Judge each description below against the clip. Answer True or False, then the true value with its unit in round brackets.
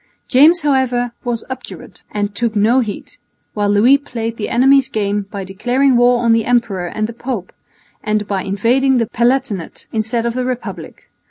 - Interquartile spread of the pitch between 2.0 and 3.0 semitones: False (3.4 semitones)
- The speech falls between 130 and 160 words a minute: False (170 wpm)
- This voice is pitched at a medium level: False (235 Hz)